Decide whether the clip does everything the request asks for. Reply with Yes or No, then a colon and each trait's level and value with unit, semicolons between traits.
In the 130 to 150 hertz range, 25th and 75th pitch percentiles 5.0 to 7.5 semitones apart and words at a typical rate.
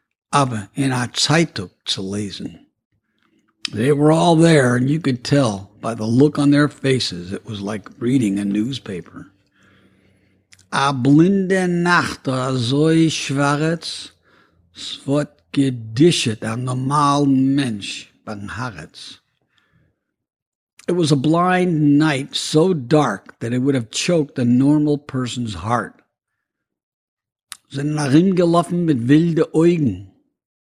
No: medium, 140 Hz; wide, 5.5 semitones; slow, 110 wpm